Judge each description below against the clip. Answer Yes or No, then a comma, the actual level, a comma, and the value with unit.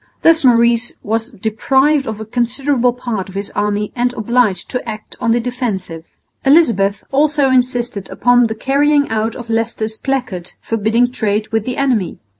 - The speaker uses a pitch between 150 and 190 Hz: No, high, 235 Hz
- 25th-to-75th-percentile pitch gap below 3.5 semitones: Yes, average, 2.8 semitones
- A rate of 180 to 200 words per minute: No, average, 160 wpm